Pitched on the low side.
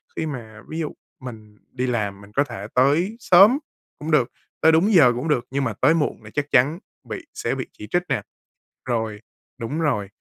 Yes: low, 130 Hz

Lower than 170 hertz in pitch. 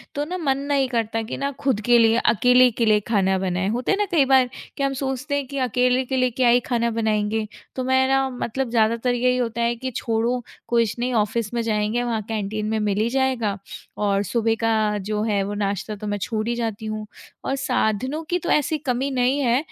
No: high, 235 Hz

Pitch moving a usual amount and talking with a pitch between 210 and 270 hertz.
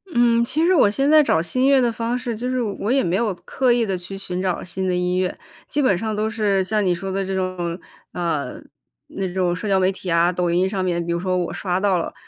No: average, 4.4 semitones; high, 190 Hz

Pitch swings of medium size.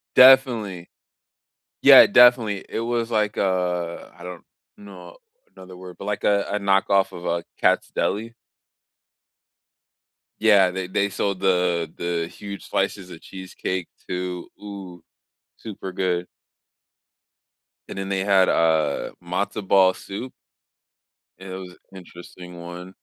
No: narrow, 2.2 semitones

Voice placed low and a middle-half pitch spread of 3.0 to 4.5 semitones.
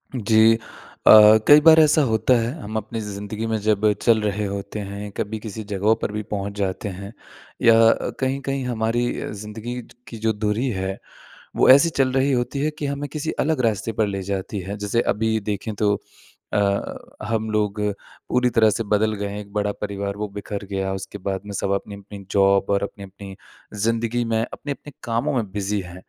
No: low, 105 Hz; narrow, 2.5 semitones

